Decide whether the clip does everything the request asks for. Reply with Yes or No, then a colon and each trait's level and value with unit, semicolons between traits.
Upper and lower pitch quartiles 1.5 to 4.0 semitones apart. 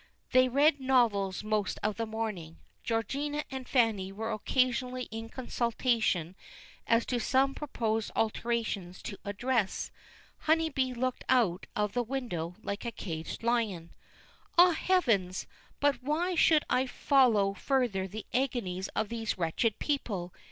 No: average, 4.4 semitones